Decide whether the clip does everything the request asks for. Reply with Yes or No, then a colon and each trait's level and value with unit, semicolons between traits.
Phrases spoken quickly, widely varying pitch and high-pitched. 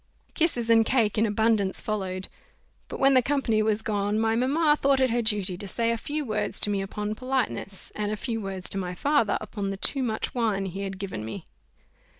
No: fast, 210 wpm; average, 3.5 semitones; high, 215 Hz